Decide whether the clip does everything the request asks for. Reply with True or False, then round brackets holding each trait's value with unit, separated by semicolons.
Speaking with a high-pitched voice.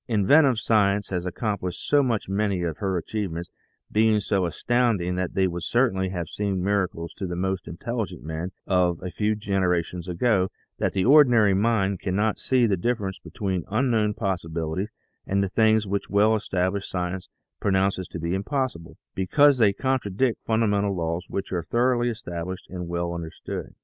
False (100 Hz)